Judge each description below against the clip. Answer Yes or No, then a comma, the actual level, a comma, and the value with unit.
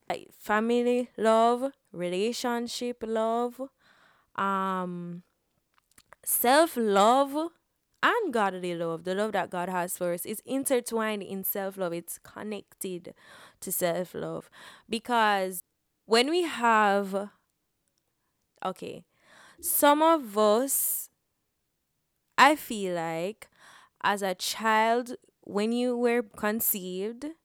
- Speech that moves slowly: Yes, slow, 100 wpm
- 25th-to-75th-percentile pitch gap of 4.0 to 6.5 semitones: Yes, average, 4.3 semitones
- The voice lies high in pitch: Yes, high, 215 Hz